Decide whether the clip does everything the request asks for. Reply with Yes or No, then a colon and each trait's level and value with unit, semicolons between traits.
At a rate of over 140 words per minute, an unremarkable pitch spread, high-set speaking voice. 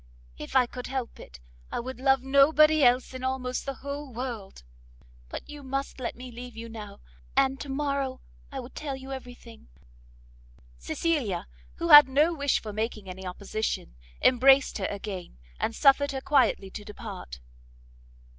Yes: average, 165 wpm; average, 3.8 semitones; very high, 255 Hz